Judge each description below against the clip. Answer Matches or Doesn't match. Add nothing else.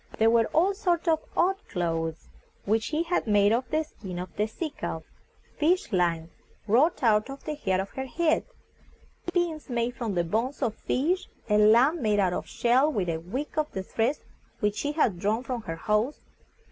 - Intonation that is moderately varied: Doesn't match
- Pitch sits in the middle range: Doesn't match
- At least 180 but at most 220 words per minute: Matches